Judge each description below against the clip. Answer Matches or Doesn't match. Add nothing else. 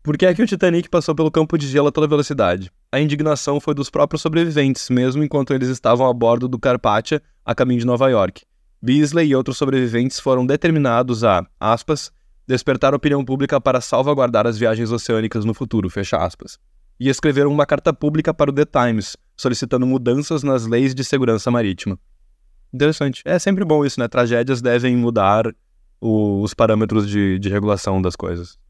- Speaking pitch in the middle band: Doesn't match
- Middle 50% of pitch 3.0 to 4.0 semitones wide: Doesn't match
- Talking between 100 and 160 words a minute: Doesn't match